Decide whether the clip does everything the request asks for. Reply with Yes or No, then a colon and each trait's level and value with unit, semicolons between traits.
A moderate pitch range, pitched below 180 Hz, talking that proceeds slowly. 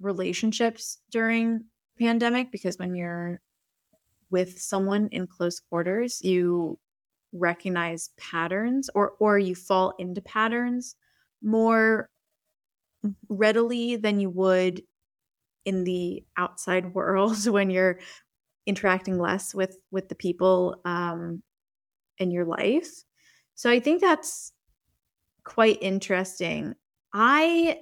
No: average, 3.8 semitones; high, 195 Hz; slow, 105 wpm